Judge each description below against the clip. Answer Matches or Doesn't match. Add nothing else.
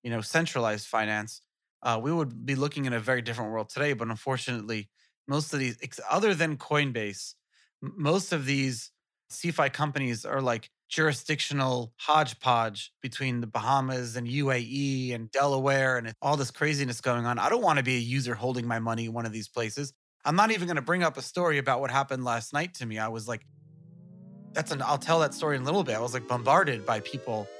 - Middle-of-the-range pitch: Doesn't match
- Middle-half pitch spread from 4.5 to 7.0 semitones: Doesn't match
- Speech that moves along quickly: Matches